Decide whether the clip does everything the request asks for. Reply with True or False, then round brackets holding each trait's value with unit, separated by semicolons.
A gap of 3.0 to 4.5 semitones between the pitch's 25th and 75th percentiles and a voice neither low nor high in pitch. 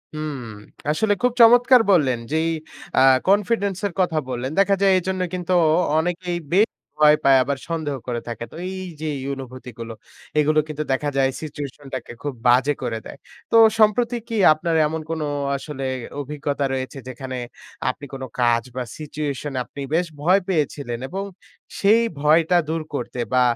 False (5.4 semitones; 150 Hz)